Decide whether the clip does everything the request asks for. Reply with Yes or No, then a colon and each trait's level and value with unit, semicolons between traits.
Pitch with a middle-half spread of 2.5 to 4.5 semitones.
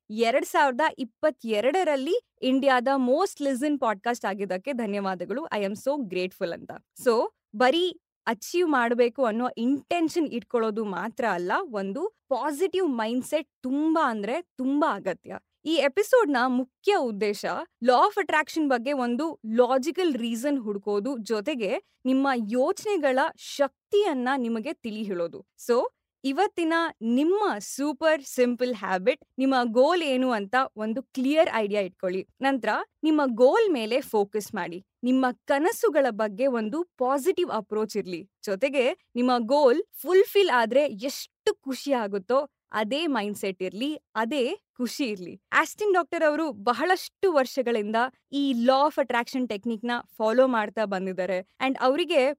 No: wide, 5.4 semitones